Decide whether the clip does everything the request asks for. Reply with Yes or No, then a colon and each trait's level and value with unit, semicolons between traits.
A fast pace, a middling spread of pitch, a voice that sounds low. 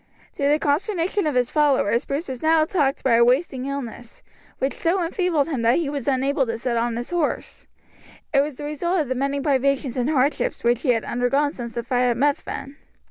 No: fast, 210 wpm; average, 3.4 semitones; very high, 275 Hz